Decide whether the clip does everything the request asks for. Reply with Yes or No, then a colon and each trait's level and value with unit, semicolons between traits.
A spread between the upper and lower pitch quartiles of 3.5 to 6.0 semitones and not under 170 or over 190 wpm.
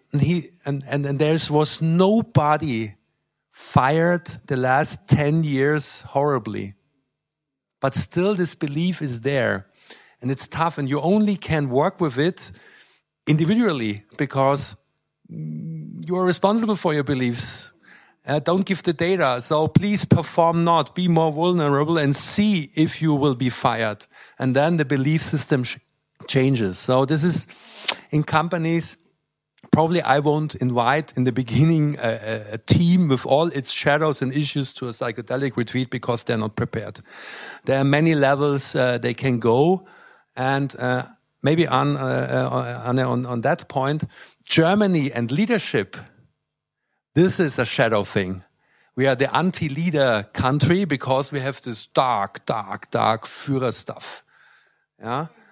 No: average, 4.2 semitones; average, 145 wpm